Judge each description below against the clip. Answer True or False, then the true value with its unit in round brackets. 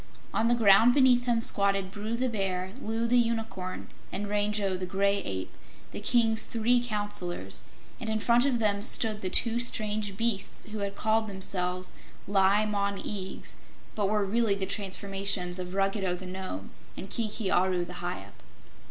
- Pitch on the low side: False (205 Hz)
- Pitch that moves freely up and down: False (2.8 semitones)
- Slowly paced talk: False (165 wpm)